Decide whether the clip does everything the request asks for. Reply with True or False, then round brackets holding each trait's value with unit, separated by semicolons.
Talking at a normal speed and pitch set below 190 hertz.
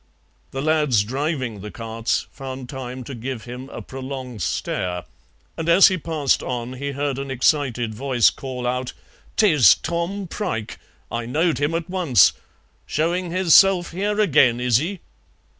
True (150 wpm; 135 Hz)